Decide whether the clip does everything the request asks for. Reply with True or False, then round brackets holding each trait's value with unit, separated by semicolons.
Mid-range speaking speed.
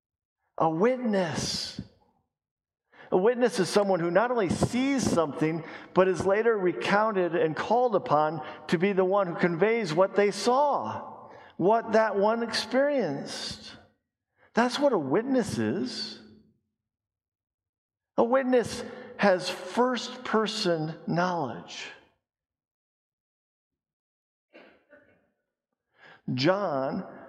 False (95 wpm)